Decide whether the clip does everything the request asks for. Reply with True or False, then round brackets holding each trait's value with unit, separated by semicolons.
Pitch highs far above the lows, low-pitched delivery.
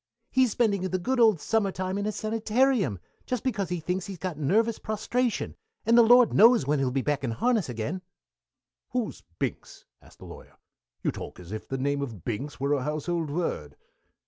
False (7.9 semitones; 185 Hz)